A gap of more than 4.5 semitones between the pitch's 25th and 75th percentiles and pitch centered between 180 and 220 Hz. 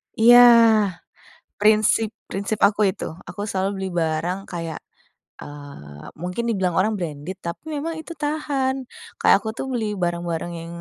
Yes: average, 4.9 semitones; high, 190 Hz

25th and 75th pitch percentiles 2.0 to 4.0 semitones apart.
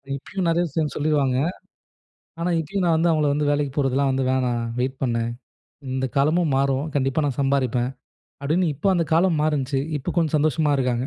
Yes: average, 3.2 semitones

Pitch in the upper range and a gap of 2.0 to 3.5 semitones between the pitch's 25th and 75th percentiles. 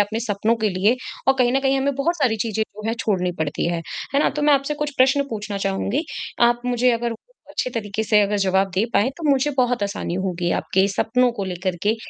No: high, 225 Hz; average, 4.7 semitones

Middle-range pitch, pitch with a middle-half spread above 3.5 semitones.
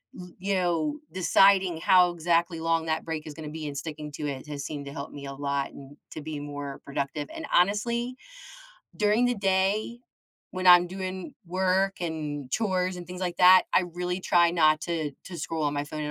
Yes: medium, 170 Hz; average, 3.9 semitones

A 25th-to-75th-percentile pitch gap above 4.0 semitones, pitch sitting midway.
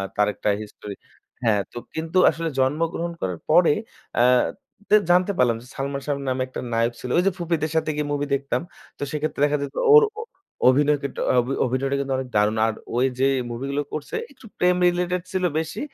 Yes: average, 4.6 semitones; medium, 145 Hz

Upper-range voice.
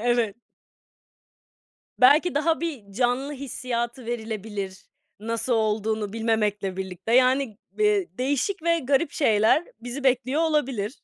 Yes: high, 245 Hz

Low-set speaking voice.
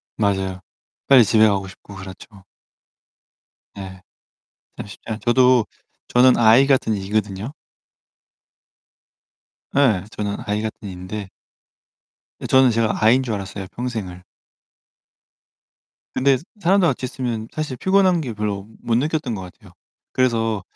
Yes: low, 110 Hz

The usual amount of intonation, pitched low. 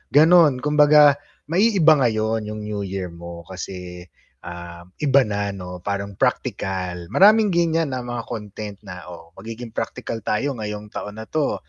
No: wide, 7.7 semitones; low, 105 Hz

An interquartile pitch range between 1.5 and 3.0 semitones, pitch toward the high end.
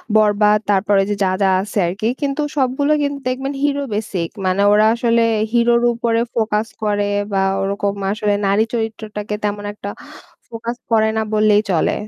Yes: narrow, 2.4 semitones; high, 215 Hz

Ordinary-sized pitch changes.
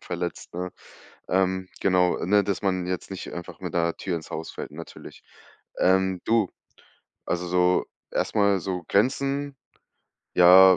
No: narrow, 1.6 semitones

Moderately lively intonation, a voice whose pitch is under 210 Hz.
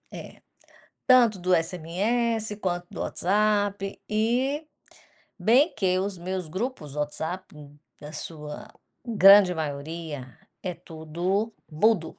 Yes: average, 4.7 semitones; medium, 185 Hz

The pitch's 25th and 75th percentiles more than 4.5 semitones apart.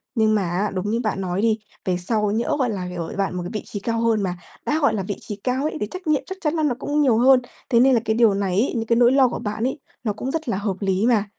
No: average, 4.1 semitones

